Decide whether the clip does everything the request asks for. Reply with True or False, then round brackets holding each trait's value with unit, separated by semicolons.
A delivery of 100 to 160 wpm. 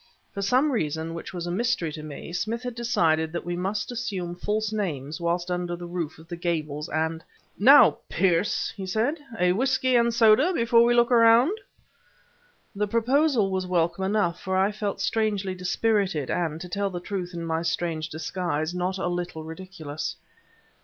False (175 wpm)